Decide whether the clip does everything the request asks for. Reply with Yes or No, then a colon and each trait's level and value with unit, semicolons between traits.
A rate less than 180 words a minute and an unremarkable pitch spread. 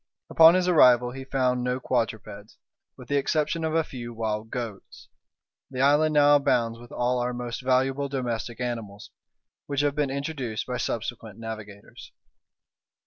Yes: average, 150 wpm; average, 3.5 semitones